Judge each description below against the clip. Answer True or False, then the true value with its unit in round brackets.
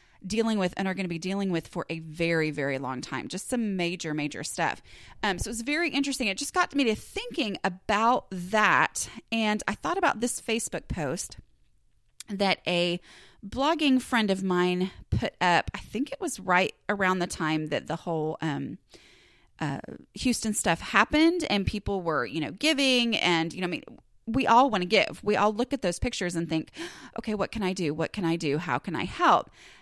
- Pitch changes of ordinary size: False (6.2 semitones)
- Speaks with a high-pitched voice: True (195 Hz)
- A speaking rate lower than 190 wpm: False (205 wpm)